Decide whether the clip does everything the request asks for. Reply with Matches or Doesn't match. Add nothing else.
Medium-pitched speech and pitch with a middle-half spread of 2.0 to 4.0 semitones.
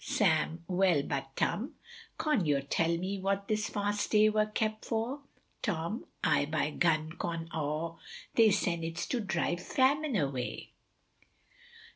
Doesn't match